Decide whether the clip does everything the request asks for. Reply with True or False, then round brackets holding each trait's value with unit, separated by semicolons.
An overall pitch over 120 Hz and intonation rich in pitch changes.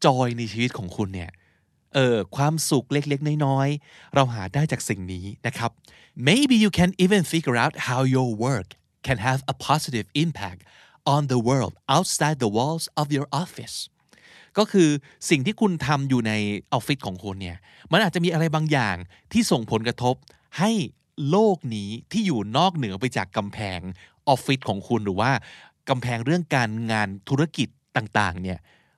True (130 Hz; 5.9 semitones)